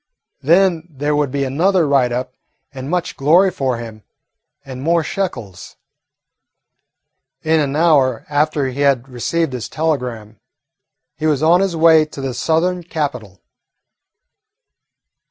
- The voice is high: No, medium, 145 Hz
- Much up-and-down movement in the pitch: No, average, 4.1 semitones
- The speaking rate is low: Yes, slow, 130 wpm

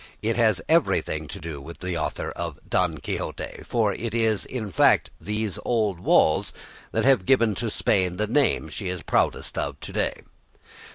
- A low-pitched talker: Yes, low, 105 Hz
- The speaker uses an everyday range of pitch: Yes, average, 4.2 semitones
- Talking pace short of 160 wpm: No, average, 175 wpm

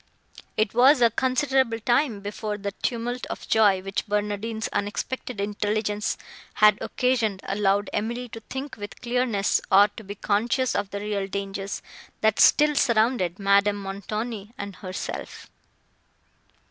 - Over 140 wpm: No, slow, 135 wpm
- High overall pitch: Yes, high, 210 Hz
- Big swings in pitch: No, average, 3.0 semitones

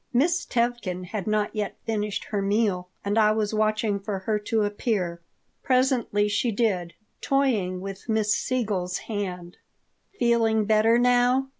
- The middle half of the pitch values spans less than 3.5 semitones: Yes, average, 2.9 semitones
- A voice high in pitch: Yes, high, 215 Hz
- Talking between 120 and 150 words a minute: Yes, average, 140 wpm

